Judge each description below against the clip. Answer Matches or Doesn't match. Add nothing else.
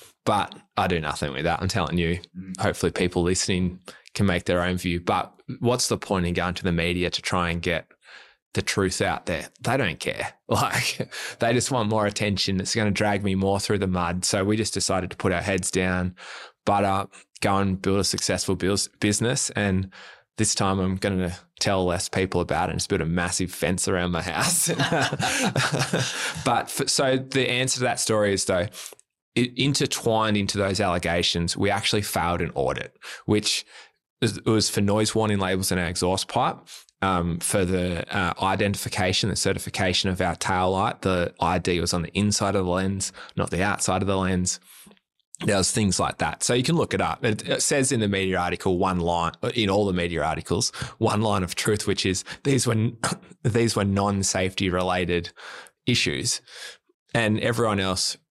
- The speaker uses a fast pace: Doesn't match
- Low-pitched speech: Matches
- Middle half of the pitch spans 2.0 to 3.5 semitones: Matches